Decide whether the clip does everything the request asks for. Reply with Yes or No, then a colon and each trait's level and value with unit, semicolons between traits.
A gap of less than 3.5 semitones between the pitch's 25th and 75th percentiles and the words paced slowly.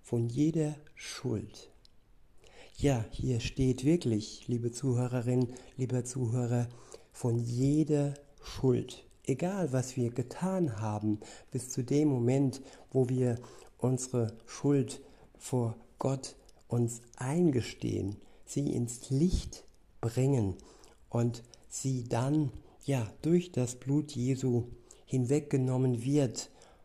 Yes: narrow, 2.6 semitones; slow, 100 wpm